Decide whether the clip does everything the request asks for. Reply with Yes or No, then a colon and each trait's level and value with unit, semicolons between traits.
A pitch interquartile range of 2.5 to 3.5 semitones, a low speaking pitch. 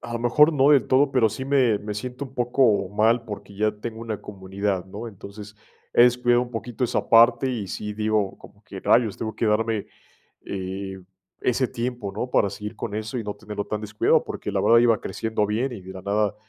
Yes: average, 2.9 semitones; low, 110 Hz